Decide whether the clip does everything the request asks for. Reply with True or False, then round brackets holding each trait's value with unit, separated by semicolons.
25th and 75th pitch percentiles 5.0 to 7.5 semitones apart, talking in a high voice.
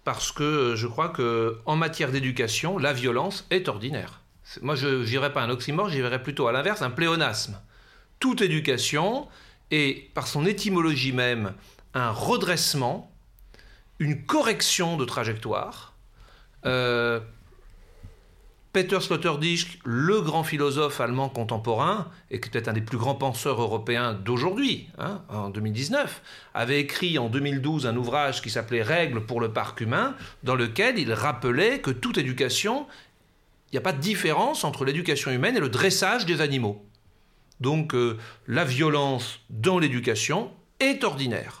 False (5.3 semitones; 135 Hz)